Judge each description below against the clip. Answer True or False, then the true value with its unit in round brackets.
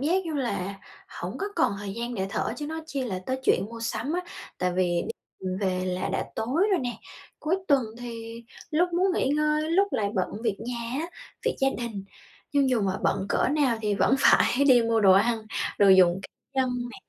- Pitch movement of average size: False (6.4 semitones)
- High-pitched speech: True (235 Hz)